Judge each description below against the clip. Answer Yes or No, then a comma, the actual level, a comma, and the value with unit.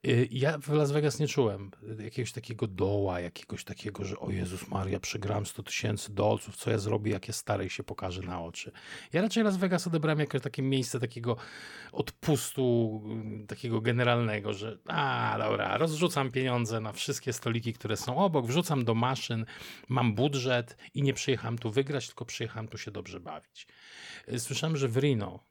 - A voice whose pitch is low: Yes, low, 120 Hz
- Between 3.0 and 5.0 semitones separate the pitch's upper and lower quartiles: Yes, average, 4.2 semitones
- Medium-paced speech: No, fast, 170 wpm